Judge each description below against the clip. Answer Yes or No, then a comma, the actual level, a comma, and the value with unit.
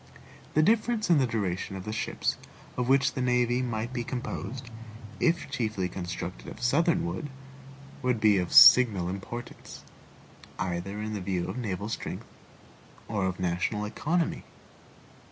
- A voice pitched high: No, low, 115 Hz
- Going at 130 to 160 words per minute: Yes, average, 145 wpm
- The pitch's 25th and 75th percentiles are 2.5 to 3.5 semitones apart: No, average, 5.1 semitones